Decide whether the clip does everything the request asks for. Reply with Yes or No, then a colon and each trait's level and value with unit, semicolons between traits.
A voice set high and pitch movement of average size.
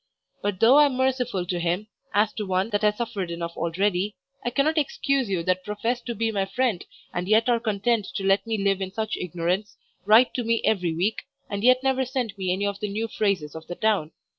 Yes: high, 210 Hz; average, 4.0 semitones